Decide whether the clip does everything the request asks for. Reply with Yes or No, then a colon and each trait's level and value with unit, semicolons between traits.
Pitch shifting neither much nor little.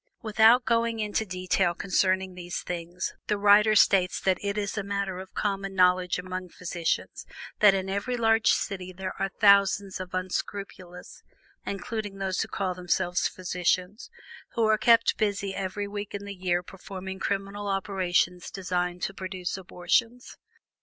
No: narrow, 2.0 semitones